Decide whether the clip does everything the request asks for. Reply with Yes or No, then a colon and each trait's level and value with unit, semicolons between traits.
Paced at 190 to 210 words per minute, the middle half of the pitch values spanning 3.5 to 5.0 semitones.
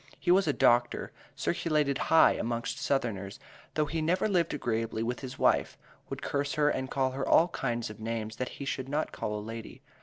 Yes: average, 195 wpm; average, 4.7 semitones